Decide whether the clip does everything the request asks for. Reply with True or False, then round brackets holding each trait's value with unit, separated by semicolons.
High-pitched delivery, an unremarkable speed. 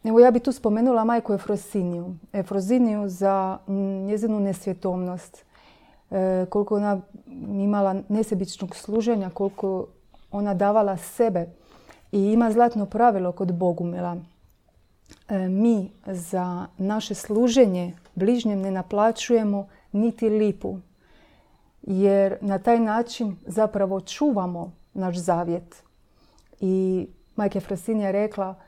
False (200 Hz; 105 wpm)